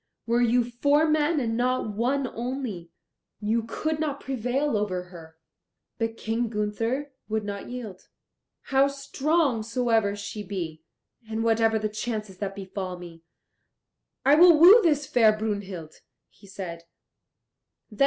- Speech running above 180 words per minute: No, slow, 135 wpm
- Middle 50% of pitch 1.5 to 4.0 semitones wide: No, average, 4.8 semitones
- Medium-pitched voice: No, high, 225 Hz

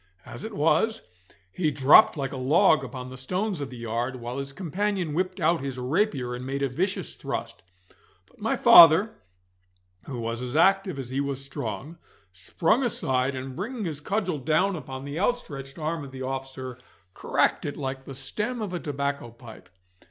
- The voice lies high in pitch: No, medium, 140 Hz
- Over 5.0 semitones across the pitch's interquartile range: Yes, wide, 5.5 semitones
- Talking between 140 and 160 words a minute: No, average, 180 wpm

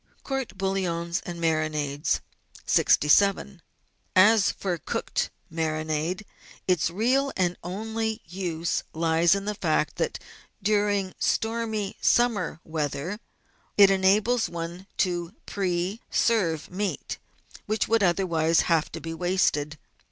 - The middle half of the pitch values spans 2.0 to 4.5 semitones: Yes, average, 3.8 semitones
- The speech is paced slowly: Yes, slow, 110 wpm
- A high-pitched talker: No, medium, 180 Hz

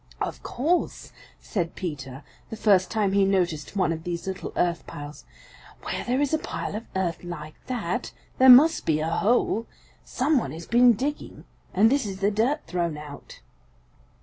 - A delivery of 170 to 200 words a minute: Yes, average, 175 wpm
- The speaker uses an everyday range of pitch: No, wide, 6.4 semitones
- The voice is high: Yes, high, 195 Hz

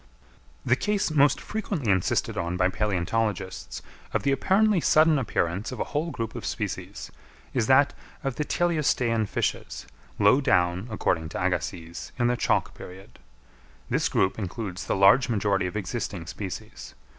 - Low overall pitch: Yes, low, 110 Hz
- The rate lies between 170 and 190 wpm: No, average, 150 wpm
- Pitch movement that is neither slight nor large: No, wide, 6.7 semitones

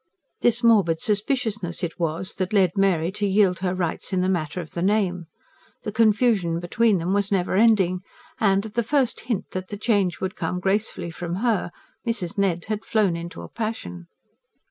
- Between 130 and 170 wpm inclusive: No, average, 185 wpm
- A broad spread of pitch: No, average, 3.5 semitones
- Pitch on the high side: Yes, high, 195 Hz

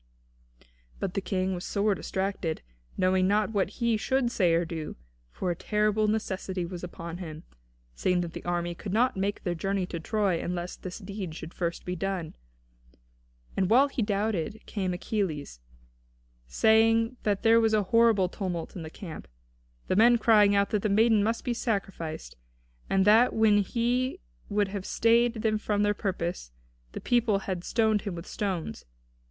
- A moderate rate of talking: Yes, average, 170 wpm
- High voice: Yes, high, 200 Hz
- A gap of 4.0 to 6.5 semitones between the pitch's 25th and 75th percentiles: No, average, 3.5 semitones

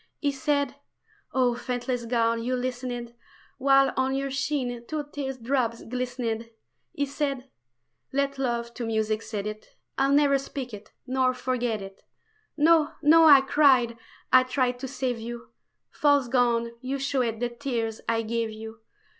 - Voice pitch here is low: No, very high, 255 Hz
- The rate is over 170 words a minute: No, average, 150 wpm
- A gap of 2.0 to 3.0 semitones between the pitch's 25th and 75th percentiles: Yes, average, 2.7 semitones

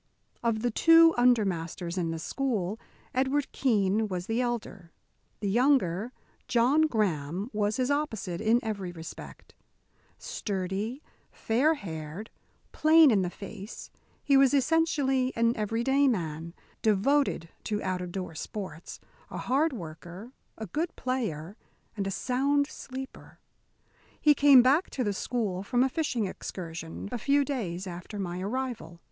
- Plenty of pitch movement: Yes, wide, 6.3 semitones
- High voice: Yes, high, 220 Hz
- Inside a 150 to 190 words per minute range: No, average, 140 wpm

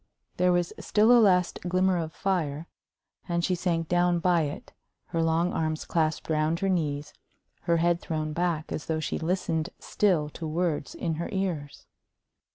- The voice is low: No, medium, 170 Hz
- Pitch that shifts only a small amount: Yes, narrow, 2.3 semitones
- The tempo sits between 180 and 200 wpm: No, average, 165 wpm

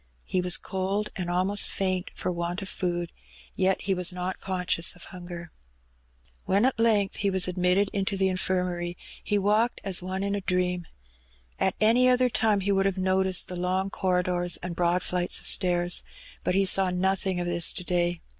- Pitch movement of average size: No, narrow, 1.5 semitones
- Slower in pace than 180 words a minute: No, average, 185 wpm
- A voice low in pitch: No, medium, 185 Hz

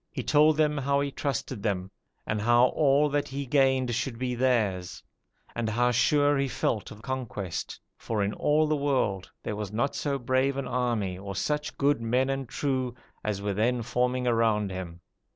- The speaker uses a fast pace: No, average, 185 wpm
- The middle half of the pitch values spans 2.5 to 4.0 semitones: No, average, 4.4 semitones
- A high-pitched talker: No, low, 125 Hz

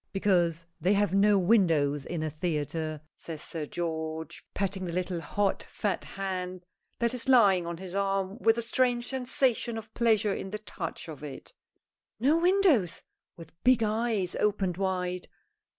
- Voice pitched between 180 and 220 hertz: Yes, high, 190 Hz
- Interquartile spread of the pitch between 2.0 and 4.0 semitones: No, average, 4.6 semitones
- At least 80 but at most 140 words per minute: No, average, 155 wpm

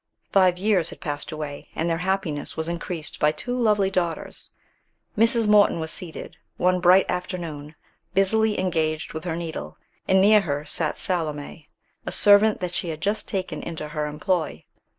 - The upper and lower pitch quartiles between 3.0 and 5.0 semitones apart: Yes, average, 3.7 semitones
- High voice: No, medium, 175 Hz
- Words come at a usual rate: Yes, average, 165 wpm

